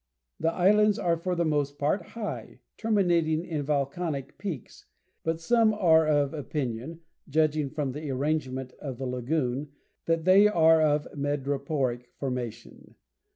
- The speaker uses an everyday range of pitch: Yes, average, 3.4 semitones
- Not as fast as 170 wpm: Yes, slow, 135 wpm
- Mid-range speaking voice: Yes, medium, 155 Hz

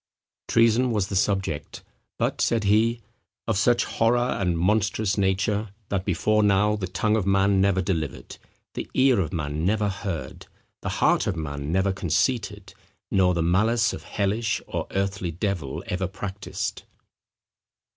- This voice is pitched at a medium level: No, low, 100 Hz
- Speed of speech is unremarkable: Yes, average, 145 wpm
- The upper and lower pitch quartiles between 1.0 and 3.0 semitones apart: Yes, average, 2.7 semitones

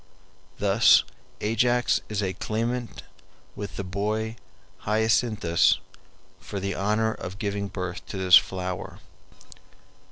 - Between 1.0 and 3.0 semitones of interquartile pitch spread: Yes, narrow, 2.6 semitones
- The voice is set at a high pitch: No, low, 105 Hz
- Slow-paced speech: Yes, slow, 105 wpm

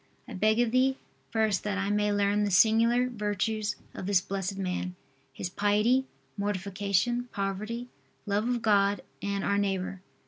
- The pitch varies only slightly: Yes, narrow, 2.1 semitones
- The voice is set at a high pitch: Yes, high, 205 Hz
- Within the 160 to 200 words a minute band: No, average, 150 wpm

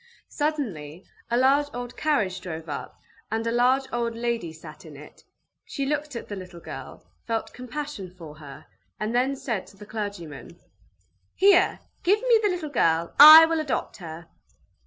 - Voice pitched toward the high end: Yes, high, 230 Hz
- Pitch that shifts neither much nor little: No, wide, 9.0 semitones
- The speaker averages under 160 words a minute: No, average, 165 wpm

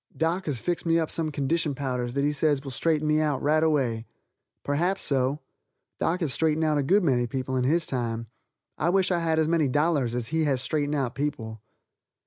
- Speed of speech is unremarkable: No, fast, 210 wpm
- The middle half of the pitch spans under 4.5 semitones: Yes, average, 3.6 semitones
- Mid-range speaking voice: Yes, medium, 150 Hz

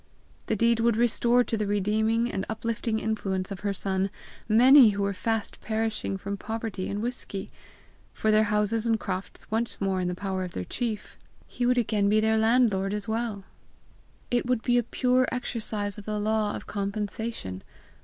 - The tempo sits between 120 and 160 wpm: No, average, 180 wpm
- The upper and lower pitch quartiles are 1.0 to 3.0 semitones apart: Yes, narrow, 2.5 semitones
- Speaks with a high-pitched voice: Yes, high, 215 Hz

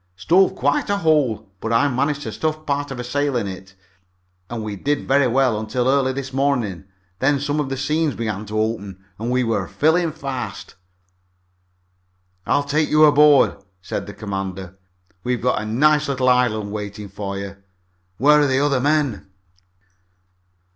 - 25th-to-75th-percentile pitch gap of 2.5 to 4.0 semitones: No, average, 5.1 semitones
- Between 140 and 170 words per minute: Yes, average, 165 wpm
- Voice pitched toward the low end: Yes, low, 130 Hz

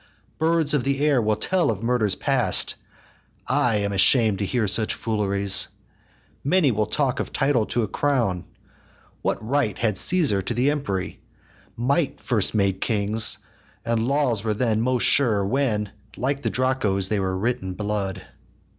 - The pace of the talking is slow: No, average, 160 wpm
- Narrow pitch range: No, average, 4.9 semitones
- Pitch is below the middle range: Yes, low, 115 Hz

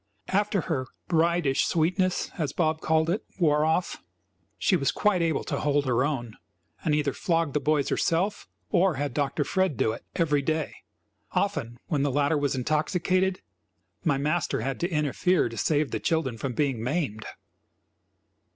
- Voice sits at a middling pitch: Yes, medium, 155 Hz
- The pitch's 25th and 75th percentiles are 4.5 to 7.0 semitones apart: No, average, 3.6 semitones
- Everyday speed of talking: Yes, average, 160 wpm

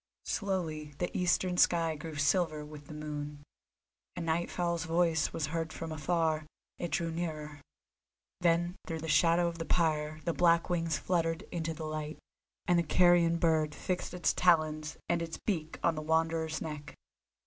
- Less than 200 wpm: Yes, average, 165 wpm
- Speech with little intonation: Yes, narrow, 1.8 semitones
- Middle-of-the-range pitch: Yes, medium, 165 Hz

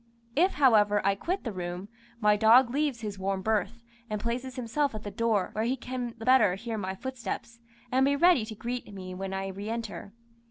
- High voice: Yes, high, 225 Hz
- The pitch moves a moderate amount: Yes, average, 4.0 semitones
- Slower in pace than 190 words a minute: No, fast, 205 wpm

